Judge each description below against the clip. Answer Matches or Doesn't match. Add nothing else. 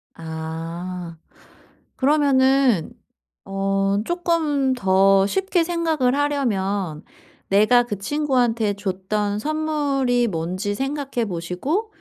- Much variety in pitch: Matches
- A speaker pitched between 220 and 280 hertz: Matches